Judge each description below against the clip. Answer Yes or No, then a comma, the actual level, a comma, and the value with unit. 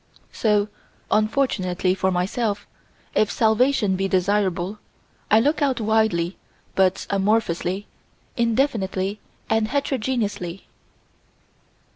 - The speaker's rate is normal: No, slow, 85 wpm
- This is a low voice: No, high, 210 Hz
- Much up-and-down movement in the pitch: No, average, 3.1 semitones